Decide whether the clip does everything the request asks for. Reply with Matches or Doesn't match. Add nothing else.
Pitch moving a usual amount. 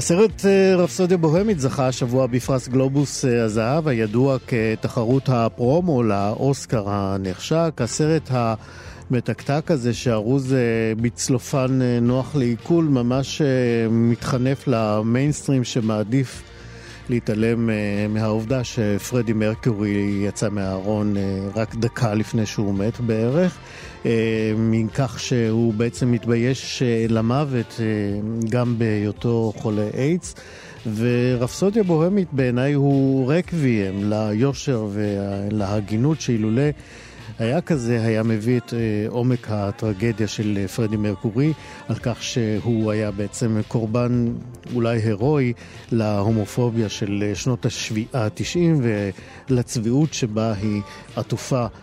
Matches